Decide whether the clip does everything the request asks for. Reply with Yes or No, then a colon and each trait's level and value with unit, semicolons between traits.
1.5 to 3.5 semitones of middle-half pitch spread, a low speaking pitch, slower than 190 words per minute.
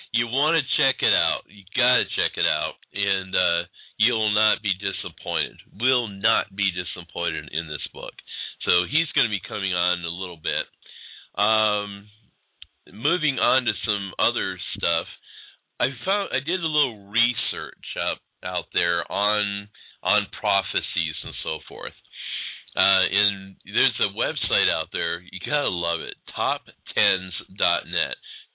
Yes: narrow, 2.5 semitones; low, 100 Hz; average, 150 wpm